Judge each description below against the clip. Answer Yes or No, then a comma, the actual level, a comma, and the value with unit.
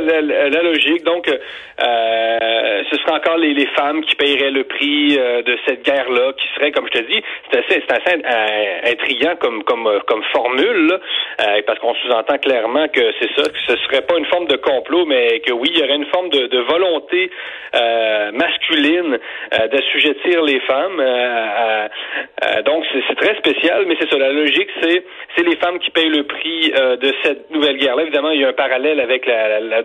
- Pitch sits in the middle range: Yes, medium, 145 Hz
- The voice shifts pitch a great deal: Yes, wide, 6.2 semitones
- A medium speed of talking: Yes, average, 210 wpm